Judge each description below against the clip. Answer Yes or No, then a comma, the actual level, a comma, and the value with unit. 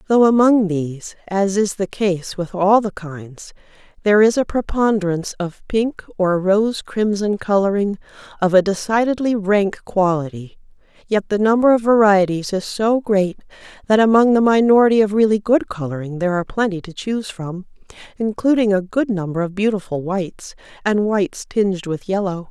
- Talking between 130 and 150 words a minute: No, average, 160 wpm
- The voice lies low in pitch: No, high, 200 Hz